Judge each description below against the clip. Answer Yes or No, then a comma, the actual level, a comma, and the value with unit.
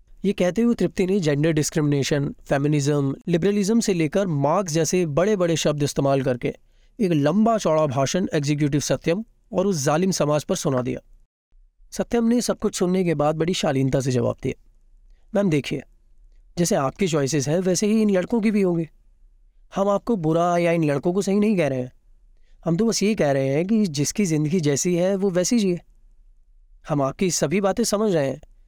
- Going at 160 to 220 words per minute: Yes, fast, 190 wpm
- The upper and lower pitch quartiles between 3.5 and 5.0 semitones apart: No, wide, 5.4 semitones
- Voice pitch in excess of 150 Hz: Yes, medium, 170 Hz